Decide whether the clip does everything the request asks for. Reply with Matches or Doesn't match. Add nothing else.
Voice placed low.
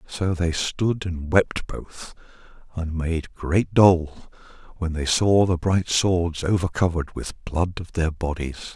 Matches